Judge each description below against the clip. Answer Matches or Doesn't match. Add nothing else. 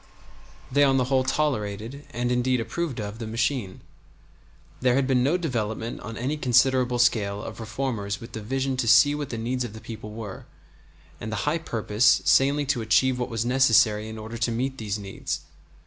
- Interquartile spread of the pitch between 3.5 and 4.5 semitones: Doesn't match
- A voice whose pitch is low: Matches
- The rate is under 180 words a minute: Doesn't match